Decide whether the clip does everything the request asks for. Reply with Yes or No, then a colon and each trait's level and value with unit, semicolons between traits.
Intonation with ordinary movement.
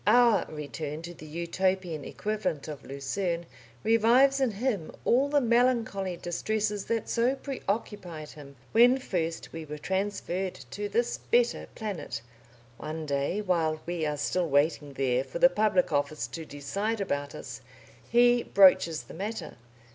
No: wide, 6.3 semitones